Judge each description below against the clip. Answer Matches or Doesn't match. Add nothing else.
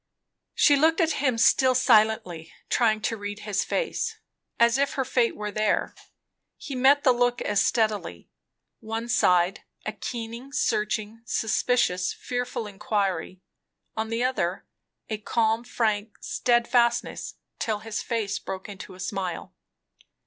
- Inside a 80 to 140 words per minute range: Matches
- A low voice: Doesn't match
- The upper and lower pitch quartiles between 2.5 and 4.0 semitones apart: Matches